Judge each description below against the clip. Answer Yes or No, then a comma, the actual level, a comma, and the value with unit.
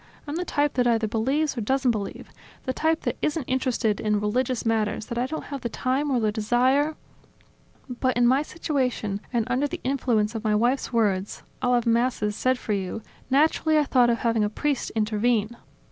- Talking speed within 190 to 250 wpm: Yes, average, 195 wpm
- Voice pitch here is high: Yes, high, 245 Hz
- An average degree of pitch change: Yes, average, 3.6 semitones